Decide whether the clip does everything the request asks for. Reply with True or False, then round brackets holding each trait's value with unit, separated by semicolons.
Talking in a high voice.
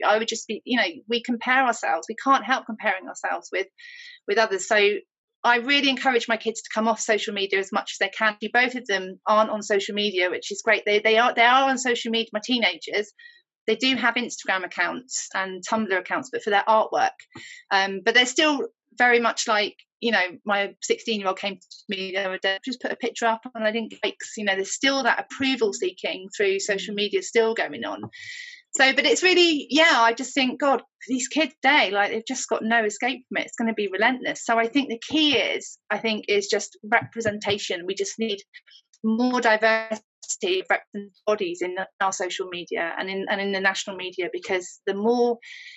True (225 Hz)